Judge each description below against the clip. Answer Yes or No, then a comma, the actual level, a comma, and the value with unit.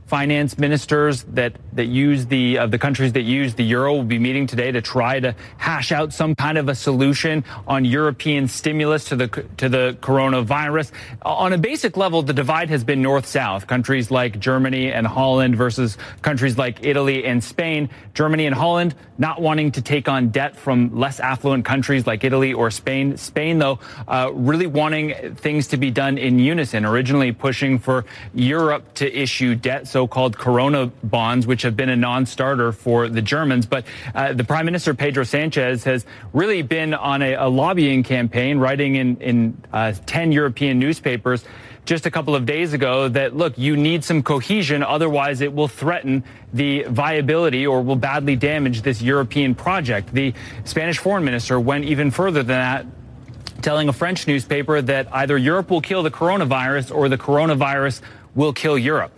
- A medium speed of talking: Yes, average, 180 wpm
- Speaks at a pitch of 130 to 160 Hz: Yes, low, 135 Hz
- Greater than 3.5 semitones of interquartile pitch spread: No, average, 2.9 semitones